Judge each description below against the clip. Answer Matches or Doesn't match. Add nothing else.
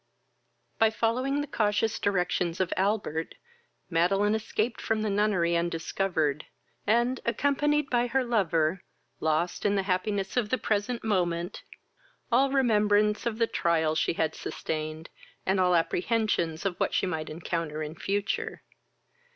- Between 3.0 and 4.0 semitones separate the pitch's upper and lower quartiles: Doesn't match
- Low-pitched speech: Doesn't match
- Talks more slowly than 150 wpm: Matches